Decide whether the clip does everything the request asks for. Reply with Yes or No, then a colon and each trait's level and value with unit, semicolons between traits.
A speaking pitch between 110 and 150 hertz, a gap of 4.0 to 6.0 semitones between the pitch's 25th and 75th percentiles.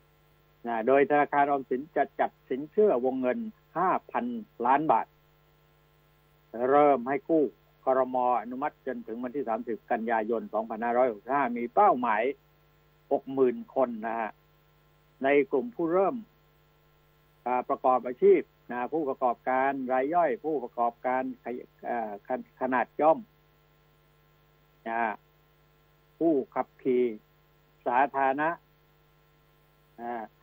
No: low, 135 Hz; average, 3.3 semitones